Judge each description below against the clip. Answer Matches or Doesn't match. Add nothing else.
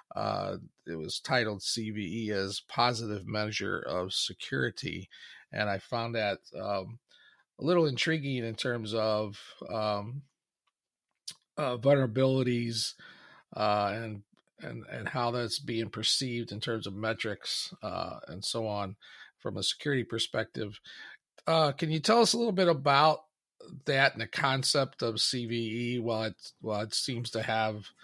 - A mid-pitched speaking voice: Doesn't match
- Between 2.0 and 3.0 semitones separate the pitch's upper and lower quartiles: Doesn't match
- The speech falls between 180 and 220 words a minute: Doesn't match